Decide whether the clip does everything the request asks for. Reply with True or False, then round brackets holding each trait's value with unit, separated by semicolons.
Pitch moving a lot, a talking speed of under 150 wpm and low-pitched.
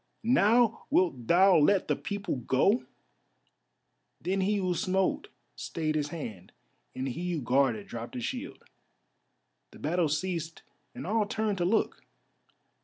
False (5.9 semitones; 135 wpm; 175 Hz)